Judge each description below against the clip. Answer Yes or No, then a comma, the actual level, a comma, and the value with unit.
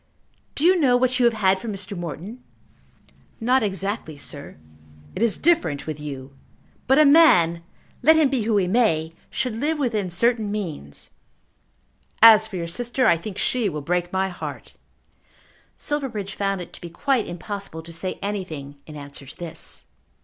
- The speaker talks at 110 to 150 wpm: No, average, 170 wpm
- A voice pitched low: No, high, 200 Hz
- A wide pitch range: Yes, wide, 6.4 semitones